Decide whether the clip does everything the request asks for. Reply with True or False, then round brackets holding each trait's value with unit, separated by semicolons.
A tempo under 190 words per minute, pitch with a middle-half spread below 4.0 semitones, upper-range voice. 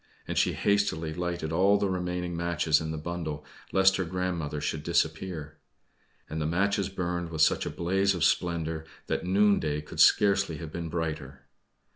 False (165 wpm; 2.9 semitones; 85 Hz)